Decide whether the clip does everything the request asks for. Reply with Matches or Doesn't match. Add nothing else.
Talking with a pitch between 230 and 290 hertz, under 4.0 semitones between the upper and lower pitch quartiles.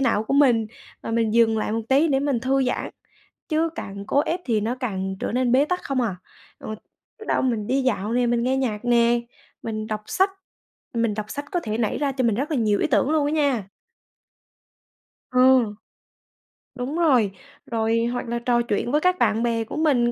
Matches